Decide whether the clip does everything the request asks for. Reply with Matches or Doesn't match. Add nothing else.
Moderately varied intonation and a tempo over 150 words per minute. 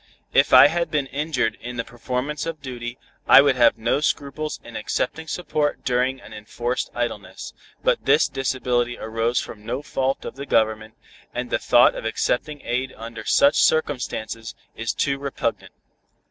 Matches